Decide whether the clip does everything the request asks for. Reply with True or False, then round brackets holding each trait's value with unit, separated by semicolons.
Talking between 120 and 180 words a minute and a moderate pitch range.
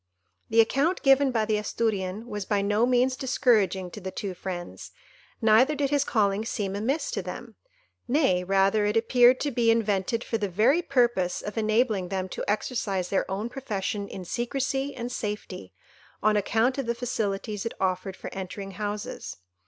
True (170 wpm; 4.0 semitones)